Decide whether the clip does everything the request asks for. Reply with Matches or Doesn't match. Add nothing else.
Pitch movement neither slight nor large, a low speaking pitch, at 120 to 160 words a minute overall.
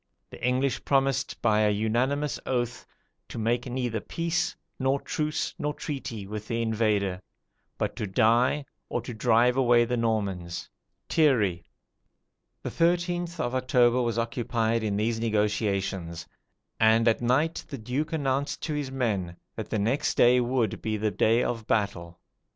Matches